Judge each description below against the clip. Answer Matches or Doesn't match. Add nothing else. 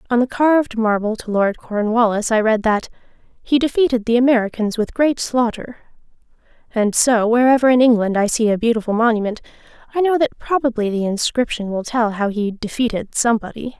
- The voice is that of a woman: Matches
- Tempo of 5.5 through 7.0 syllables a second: Matches